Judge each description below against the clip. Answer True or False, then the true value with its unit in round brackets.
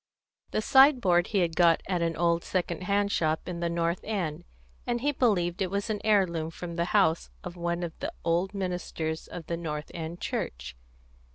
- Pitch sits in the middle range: True (175 Hz)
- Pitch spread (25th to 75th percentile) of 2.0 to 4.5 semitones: True (2.9 semitones)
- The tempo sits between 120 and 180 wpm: False (190 wpm)